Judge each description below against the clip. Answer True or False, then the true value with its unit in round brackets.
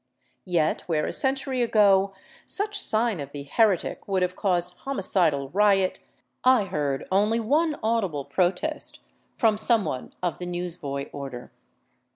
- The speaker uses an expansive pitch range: True (5.8 semitones)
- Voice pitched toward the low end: False (190 Hz)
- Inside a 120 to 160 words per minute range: True (150 wpm)